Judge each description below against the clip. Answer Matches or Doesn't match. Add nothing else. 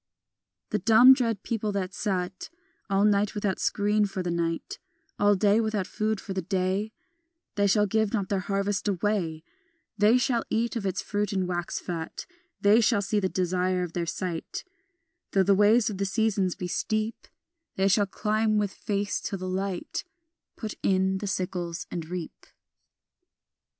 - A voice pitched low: Doesn't match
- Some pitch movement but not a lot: Doesn't match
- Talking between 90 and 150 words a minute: Doesn't match